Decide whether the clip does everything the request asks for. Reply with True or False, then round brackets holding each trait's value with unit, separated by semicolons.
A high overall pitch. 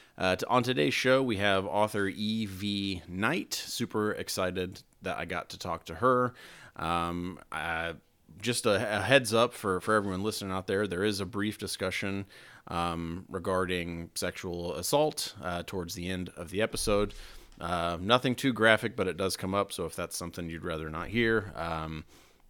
False (95 Hz)